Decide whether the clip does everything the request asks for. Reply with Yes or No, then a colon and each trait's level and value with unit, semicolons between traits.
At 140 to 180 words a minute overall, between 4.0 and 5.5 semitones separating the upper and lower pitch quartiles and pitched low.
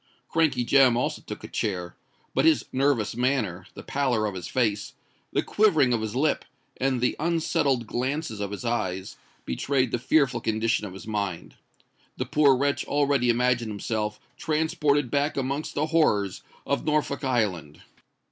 Yes: average, 155 wpm; average, 4.9 semitones; low, 125 Hz